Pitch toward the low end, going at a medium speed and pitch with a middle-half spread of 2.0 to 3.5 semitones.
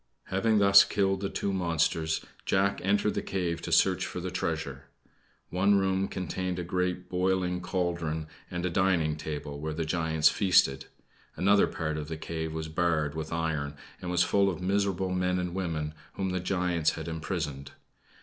Yes: very low, 90 Hz; average, 170 wpm; average, 3.0 semitones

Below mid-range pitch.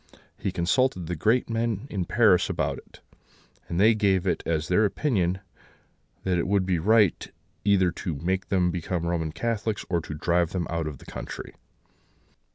Yes: very low, 90 Hz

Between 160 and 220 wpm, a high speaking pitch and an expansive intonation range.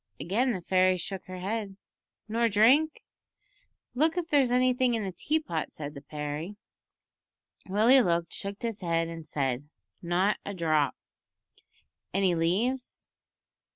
No: slow, 135 wpm; high, 195 Hz; wide, 6.2 semitones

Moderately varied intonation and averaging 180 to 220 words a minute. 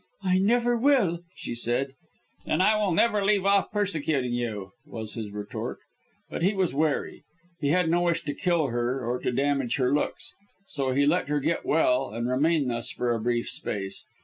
No: wide, 7.0 semitones; average, 190 wpm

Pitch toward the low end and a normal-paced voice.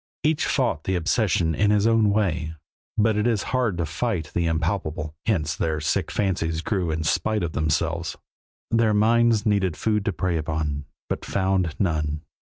Yes: very low, 90 Hz; average, 165 wpm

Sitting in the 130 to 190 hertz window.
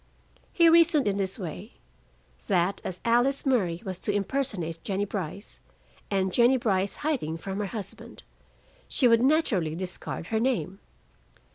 No: high, 200 Hz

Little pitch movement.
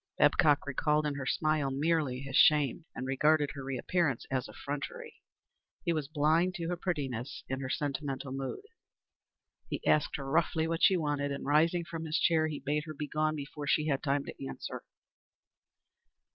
Yes: narrow, 2.3 semitones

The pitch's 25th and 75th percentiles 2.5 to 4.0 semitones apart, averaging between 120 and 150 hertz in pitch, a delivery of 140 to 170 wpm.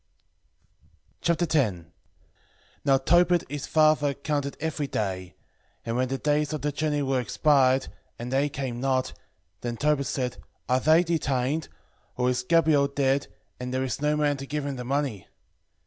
Yes: average, 2.8 semitones; medium, 140 Hz; average, 160 wpm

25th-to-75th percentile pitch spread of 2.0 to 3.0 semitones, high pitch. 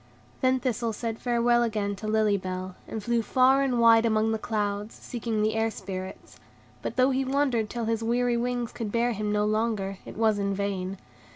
Yes: narrow, 2.4 semitones; high, 225 Hz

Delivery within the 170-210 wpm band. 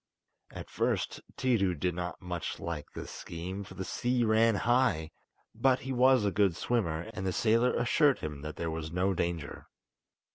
Yes: average, 175 wpm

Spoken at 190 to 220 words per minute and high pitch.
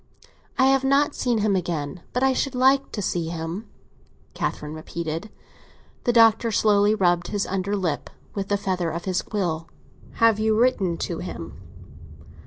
No: average, 160 wpm; high, 200 Hz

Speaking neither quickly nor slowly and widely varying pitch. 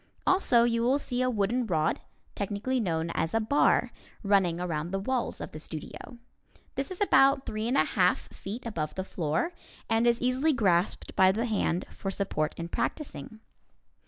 Yes: average, 175 wpm; wide, 6.1 semitones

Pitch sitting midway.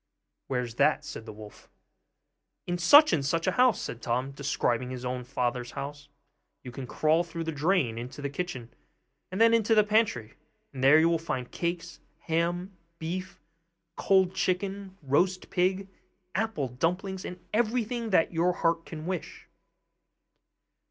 Yes: medium, 165 Hz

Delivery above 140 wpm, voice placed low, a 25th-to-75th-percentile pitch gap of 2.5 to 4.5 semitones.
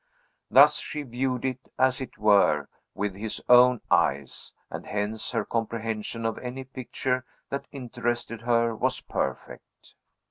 No: slow, 135 wpm; low, 120 Hz; average, 2.8 semitones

